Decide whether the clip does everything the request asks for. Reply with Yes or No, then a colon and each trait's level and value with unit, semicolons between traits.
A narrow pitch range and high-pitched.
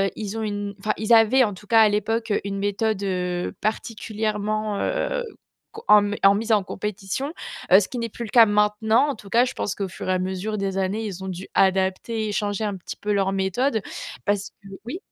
Yes: narrow, 2.3 semitones; high, 210 Hz